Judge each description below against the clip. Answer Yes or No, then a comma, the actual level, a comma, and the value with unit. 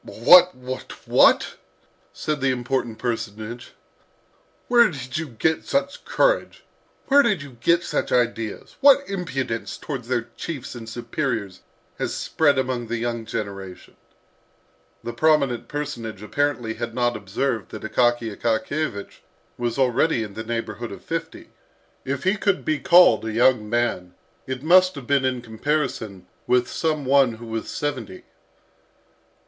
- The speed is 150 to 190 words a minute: No, average, 140 wpm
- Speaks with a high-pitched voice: No, low, 125 Hz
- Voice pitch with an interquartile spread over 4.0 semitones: Yes, average, 4.6 semitones